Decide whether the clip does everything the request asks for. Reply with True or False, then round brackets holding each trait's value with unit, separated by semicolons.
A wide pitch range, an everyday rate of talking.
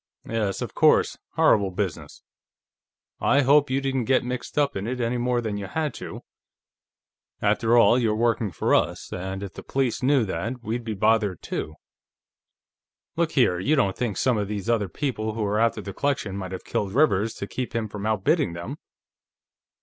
False (4.2 semitones; 185 wpm)